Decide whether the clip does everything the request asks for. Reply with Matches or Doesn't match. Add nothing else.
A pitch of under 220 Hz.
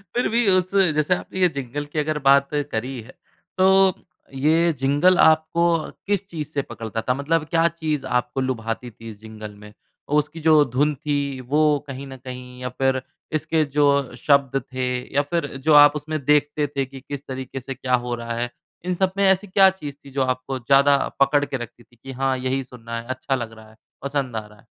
Matches